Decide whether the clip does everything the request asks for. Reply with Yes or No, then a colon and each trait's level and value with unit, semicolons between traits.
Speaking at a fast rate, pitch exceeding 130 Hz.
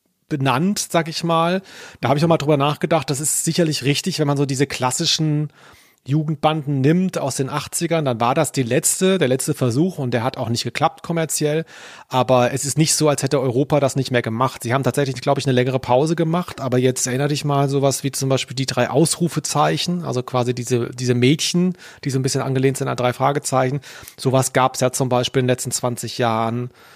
Yes: fast, 220 wpm; medium, 140 Hz